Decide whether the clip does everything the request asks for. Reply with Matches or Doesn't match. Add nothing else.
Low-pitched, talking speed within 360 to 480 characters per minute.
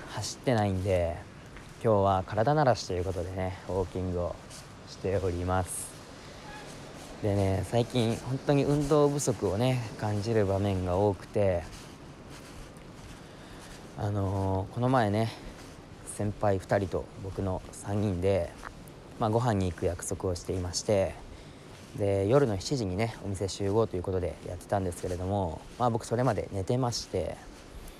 Doesn't match